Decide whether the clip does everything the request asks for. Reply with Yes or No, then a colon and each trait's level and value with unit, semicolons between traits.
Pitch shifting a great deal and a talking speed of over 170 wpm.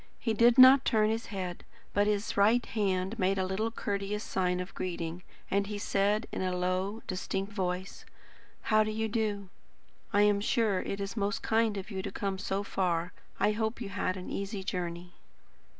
No: narrow, 2.5 semitones; average, 185 wpm